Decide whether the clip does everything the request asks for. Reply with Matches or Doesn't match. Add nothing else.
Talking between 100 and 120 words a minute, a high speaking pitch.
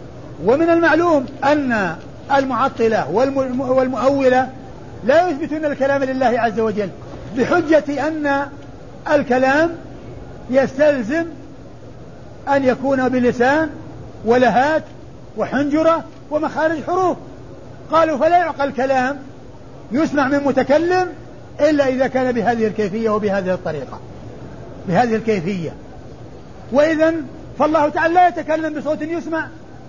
Doesn't match